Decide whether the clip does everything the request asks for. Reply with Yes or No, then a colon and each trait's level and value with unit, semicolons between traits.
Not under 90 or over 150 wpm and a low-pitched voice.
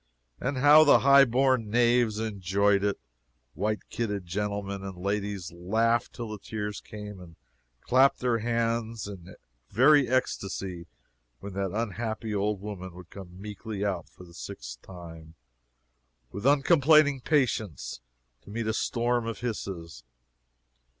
Yes: slow, 135 wpm; low, 105 Hz